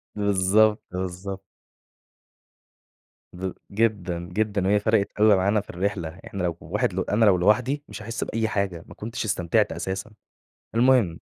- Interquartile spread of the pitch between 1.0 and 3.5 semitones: Yes, average, 2.8 semitones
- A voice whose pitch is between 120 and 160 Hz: No, low, 100 Hz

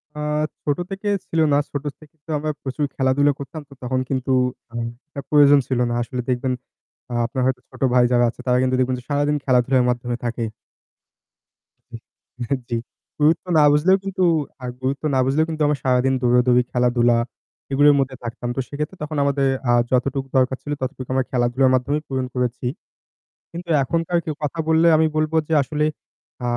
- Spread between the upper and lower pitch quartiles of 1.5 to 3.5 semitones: Yes, average, 3.0 semitones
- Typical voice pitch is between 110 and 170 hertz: Yes, low, 135 Hz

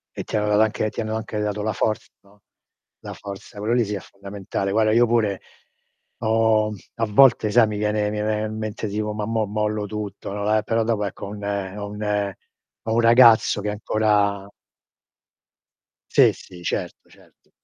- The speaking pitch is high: No, low, 105 Hz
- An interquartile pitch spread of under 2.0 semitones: Yes, narrow, 1.2 semitones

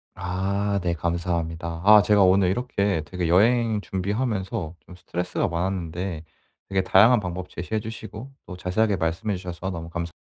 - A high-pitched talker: No, very low, 95 Hz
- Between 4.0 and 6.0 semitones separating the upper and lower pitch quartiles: No, average, 3.0 semitones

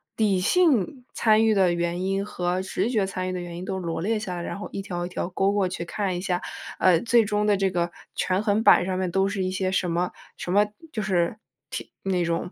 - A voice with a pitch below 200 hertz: Yes, high, 190 Hz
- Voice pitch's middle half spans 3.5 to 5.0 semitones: No, narrow, 2.5 semitones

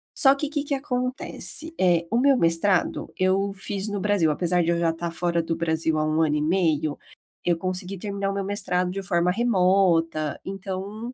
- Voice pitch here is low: No, medium, 185 Hz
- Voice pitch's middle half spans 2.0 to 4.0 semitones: Yes, average, 3.4 semitones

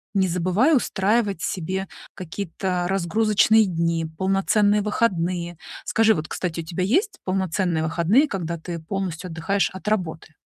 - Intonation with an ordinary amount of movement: Yes, average, 3.5 semitones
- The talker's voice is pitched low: No, high, 190 Hz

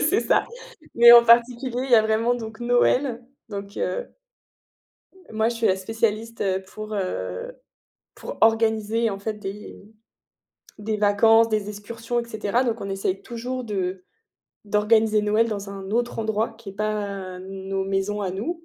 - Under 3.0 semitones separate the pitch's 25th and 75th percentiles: Yes, narrow, 2.6 semitones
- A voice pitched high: Yes, high, 215 Hz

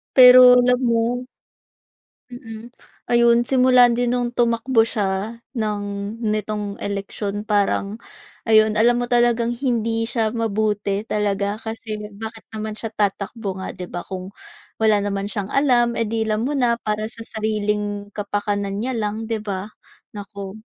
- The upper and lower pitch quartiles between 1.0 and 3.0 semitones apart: Yes, narrow, 2.4 semitones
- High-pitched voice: Yes, high, 220 Hz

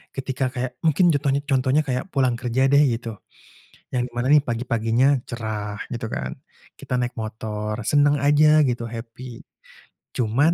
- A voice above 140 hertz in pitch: No, low, 125 Hz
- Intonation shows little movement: No, average, 3.2 semitones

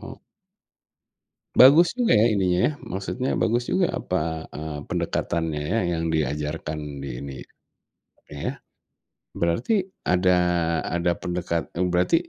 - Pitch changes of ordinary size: No, wide, 6.3 semitones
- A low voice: Yes, very low, 90 Hz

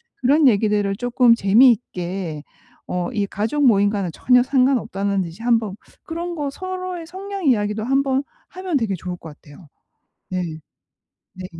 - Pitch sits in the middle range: No, high, 230 Hz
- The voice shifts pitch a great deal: Yes, wide, 6.0 semitones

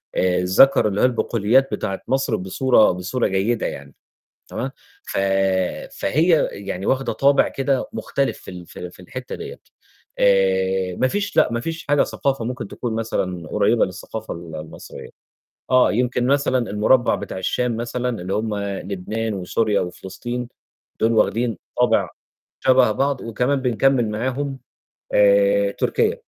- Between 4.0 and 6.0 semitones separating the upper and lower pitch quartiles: Yes, wide, 5.4 semitones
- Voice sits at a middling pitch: No, low, 115 Hz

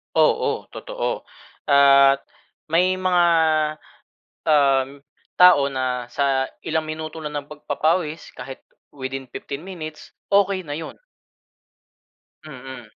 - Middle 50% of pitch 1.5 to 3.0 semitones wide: No, average, 3.4 semitones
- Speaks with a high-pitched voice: No, medium, 150 Hz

